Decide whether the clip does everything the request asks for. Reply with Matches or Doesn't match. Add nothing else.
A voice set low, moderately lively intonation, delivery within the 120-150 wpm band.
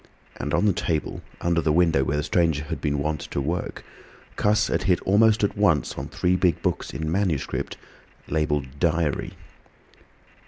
Doesn't match